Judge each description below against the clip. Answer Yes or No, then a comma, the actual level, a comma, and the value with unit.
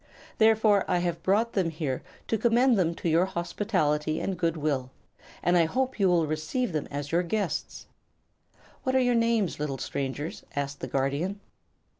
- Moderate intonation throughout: No, wide, 6.1 semitones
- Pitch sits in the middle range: Yes, medium, 175 Hz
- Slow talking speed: No, average, 170 wpm